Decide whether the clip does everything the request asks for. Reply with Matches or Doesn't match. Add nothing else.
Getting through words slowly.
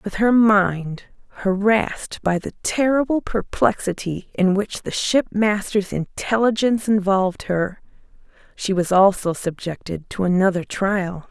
Matches